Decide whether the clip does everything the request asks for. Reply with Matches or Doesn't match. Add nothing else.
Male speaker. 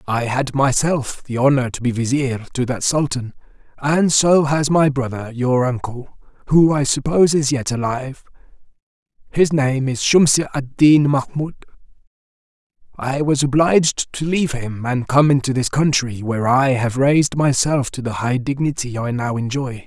Matches